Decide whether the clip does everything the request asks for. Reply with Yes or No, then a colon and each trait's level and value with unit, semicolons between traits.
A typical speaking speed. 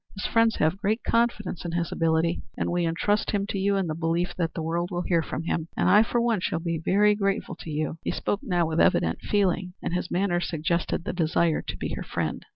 No: fast, 240 wpm